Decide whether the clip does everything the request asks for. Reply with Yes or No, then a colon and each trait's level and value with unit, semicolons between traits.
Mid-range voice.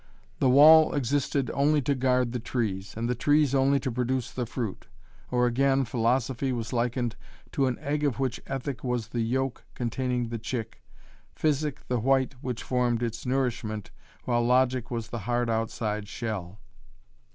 No: low, 125 Hz